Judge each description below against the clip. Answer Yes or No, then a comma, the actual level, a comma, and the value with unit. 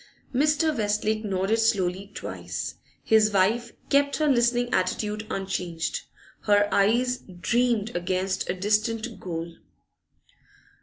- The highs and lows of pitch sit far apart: No, average, 4.0 semitones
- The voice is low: No, high, 215 Hz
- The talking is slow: Yes, slow, 105 wpm